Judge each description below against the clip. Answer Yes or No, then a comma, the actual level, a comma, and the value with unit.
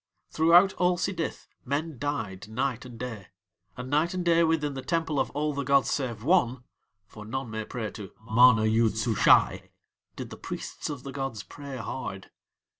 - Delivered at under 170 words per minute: No, average, 175 wpm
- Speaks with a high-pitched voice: No, low, 135 Hz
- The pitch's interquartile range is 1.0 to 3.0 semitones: No, average, 5.1 semitones